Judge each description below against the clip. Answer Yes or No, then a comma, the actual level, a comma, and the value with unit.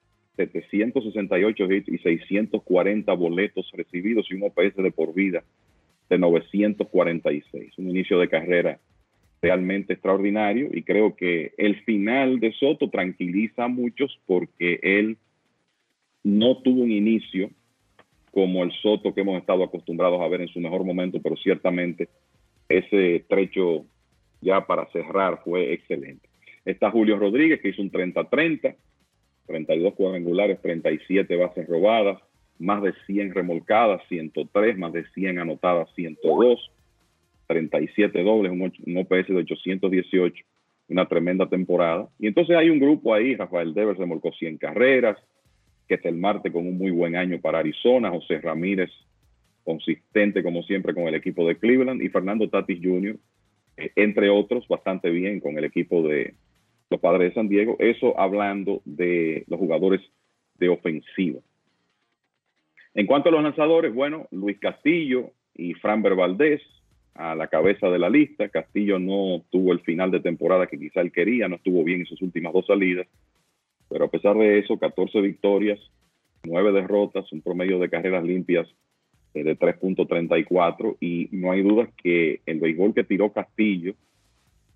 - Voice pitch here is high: No, very low, 95 Hz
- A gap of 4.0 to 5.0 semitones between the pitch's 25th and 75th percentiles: No, average, 2.8 semitones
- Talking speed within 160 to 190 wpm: No, average, 145 wpm